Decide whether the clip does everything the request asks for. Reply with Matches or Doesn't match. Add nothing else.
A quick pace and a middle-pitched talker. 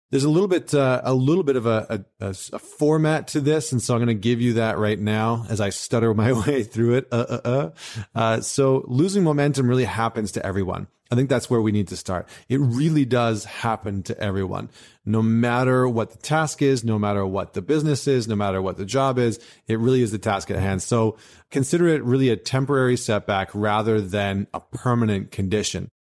Doesn't match